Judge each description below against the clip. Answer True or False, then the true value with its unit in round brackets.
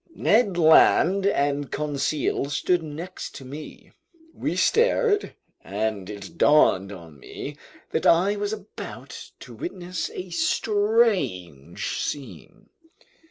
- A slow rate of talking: True (110 wpm)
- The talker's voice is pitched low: False (160 Hz)